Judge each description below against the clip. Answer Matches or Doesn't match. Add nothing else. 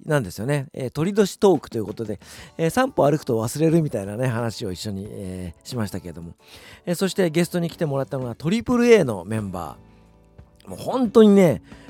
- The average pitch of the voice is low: Matches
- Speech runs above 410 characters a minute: Doesn't match